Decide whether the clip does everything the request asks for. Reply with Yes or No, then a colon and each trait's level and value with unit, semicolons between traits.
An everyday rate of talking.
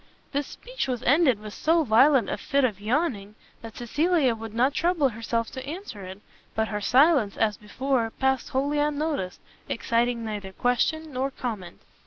Yes: average, 165 wpm